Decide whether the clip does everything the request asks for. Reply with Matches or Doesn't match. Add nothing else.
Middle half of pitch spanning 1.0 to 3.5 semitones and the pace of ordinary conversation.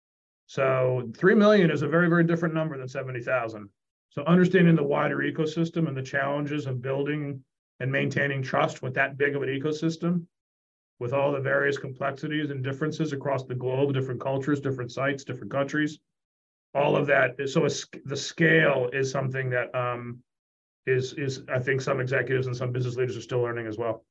Matches